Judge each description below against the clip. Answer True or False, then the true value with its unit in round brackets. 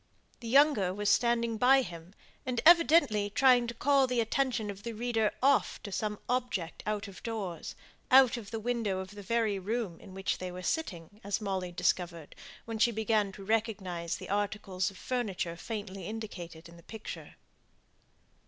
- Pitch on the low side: False (215 Hz)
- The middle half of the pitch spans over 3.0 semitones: True (3.9 semitones)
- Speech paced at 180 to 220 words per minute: False (170 wpm)